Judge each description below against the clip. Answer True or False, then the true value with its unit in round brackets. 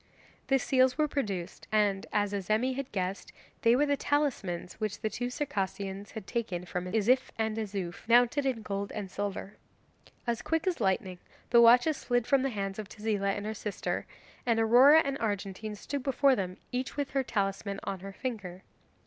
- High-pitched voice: True (220 Hz)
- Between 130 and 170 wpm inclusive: False (180 wpm)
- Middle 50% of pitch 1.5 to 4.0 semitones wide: False (4.6 semitones)